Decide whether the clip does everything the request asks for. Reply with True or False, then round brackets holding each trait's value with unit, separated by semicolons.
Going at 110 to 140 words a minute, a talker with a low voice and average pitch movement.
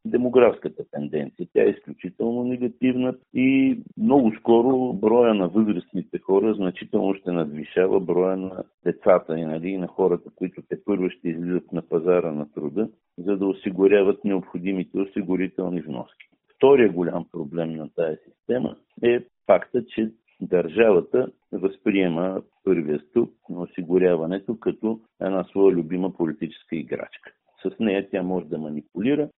True (130 wpm; 95 Hz; 4.5 semitones)